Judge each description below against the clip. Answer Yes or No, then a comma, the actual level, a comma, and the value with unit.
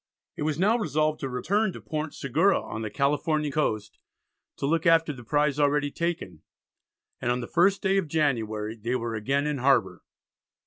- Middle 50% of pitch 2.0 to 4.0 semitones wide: No, average, 4.8 semitones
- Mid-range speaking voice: Yes, medium, 145 Hz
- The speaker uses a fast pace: No, average, 180 wpm